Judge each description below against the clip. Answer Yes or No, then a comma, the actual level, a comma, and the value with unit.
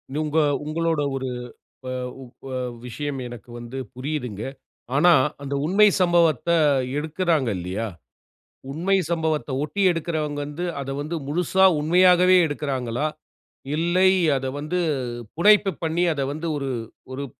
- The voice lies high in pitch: No, medium, 155 Hz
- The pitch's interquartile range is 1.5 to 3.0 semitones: No, average, 3.8 semitones